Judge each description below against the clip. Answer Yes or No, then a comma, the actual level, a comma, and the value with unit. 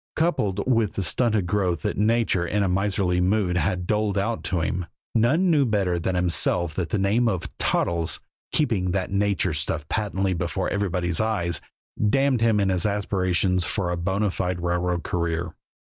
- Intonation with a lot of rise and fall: No, average, 3.0 semitones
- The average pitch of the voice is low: Yes, very low, 95 Hz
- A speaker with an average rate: Yes, average, 170 wpm